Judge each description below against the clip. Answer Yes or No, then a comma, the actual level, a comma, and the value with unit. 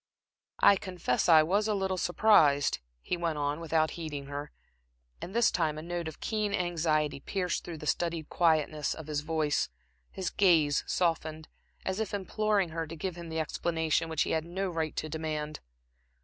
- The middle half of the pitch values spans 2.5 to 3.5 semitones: Yes, average, 2.8 semitones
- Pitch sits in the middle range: Yes, medium, 165 Hz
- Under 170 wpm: No, average, 175 wpm